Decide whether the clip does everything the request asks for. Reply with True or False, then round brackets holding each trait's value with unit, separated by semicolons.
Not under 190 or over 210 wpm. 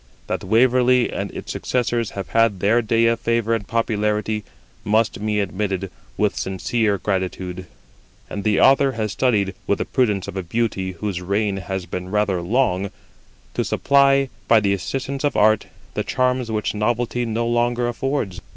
False (160 wpm)